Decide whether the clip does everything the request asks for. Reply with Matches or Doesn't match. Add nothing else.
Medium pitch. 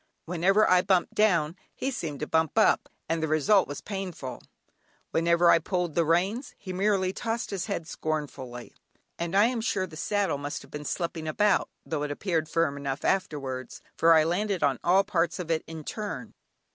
Matches